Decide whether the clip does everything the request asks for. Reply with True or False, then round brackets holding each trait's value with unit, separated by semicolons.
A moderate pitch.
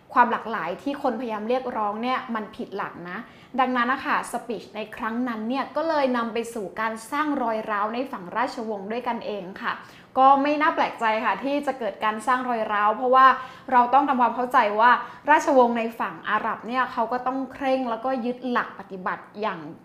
False (240 Hz)